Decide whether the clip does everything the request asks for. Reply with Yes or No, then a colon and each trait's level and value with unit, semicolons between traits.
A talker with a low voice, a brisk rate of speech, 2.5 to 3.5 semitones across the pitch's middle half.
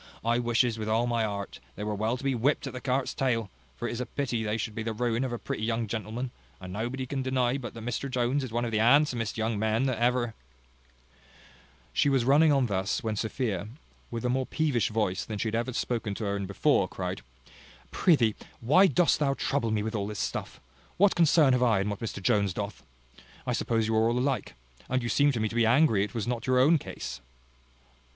Yes: low, 120 Hz; fast, 235 wpm; average, 3.0 semitones